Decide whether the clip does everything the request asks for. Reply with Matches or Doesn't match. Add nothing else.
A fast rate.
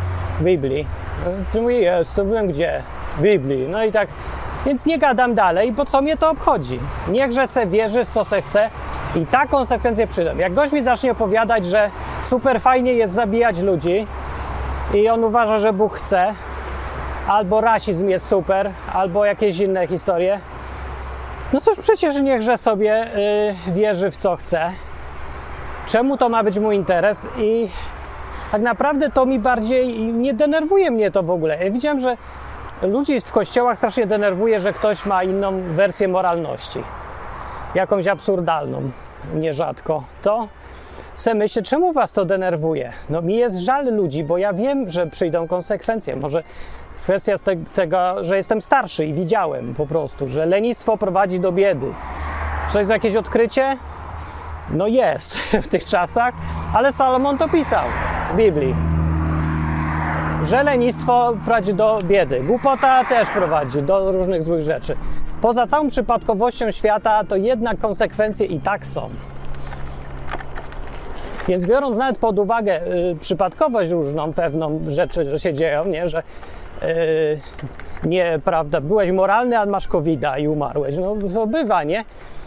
Doesn't match